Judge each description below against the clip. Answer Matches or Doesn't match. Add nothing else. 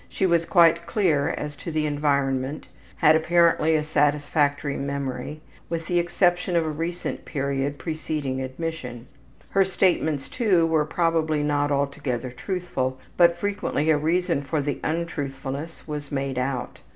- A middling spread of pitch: Matches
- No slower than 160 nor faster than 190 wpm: Doesn't match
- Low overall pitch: Doesn't match